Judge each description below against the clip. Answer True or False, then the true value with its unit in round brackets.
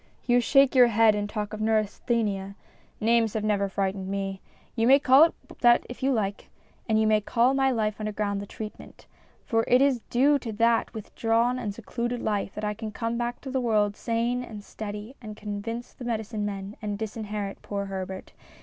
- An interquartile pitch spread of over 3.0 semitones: False (2.6 semitones)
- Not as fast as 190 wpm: False (200 wpm)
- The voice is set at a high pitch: True (220 Hz)